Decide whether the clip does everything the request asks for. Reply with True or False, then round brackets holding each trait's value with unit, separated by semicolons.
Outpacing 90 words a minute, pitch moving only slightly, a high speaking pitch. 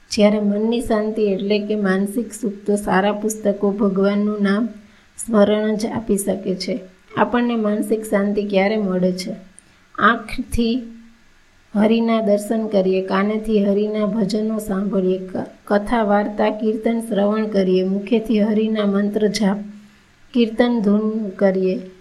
True (115 wpm; 1.7 semitones; 210 Hz)